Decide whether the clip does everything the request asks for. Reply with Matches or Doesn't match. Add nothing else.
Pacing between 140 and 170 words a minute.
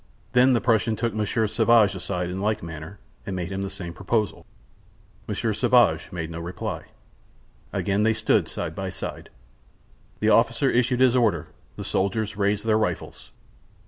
Matches